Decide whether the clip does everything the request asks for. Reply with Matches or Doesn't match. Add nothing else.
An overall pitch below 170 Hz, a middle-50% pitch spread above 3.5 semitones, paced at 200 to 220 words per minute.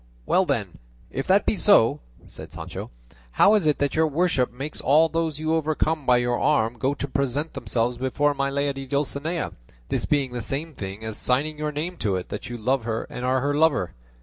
Matches